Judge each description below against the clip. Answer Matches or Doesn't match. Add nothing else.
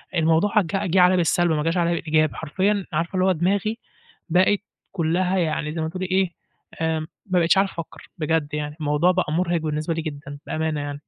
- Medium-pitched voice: Matches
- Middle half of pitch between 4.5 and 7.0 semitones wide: Doesn't match